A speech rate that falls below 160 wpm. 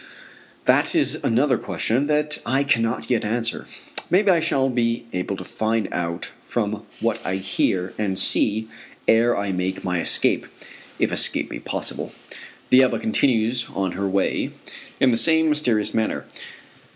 Yes: average, 150 wpm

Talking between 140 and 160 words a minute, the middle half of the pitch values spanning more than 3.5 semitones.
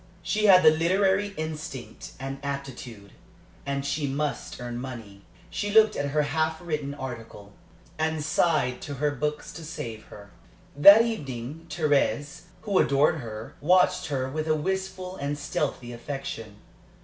Yes: average, 145 wpm; average, 4.0 semitones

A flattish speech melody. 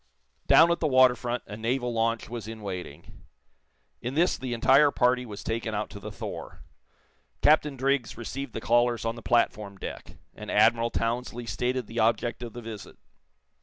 Yes: narrow, 2.2 semitones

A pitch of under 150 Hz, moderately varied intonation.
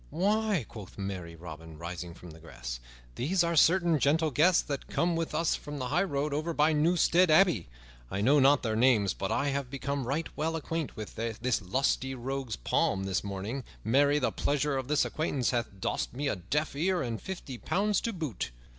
No: medium, 140 Hz; wide, 6.7 semitones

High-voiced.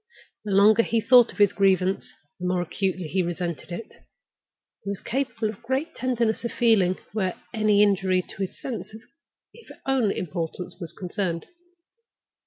Yes: high, 200 Hz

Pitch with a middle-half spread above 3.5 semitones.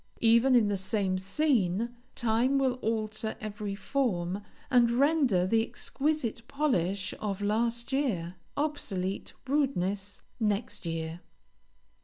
Yes: average, 4.8 semitones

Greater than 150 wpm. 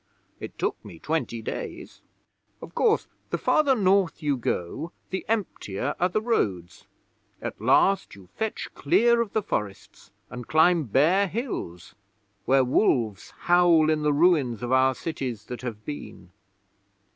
No: average, 145 wpm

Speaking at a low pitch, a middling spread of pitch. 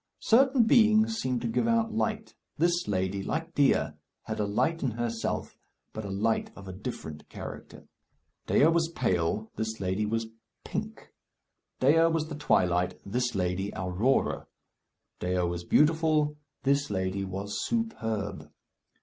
No: low, 115 Hz; wide, 9.0 semitones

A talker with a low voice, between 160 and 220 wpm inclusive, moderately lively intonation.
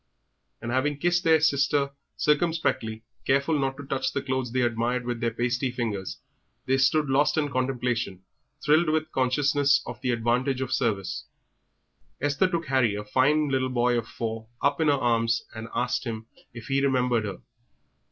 Yes: low, 130 Hz; average, 170 wpm; average, 3.3 semitones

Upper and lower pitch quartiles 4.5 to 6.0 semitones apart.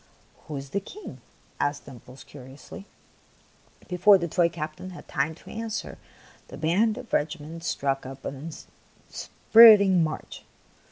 Yes: wide, 5.6 semitones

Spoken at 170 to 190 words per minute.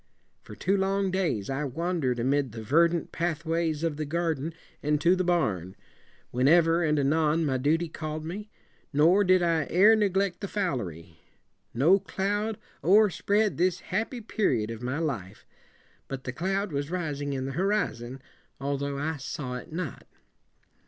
Yes: average, 180 wpm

